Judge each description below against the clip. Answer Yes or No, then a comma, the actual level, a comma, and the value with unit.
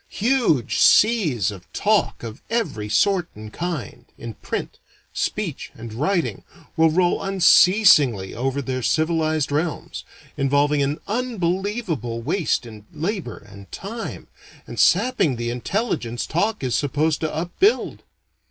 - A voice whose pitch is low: No, medium, 155 Hz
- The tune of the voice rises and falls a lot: Yes, wide, 8.2 semitones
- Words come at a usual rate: No, slow, 125 wpm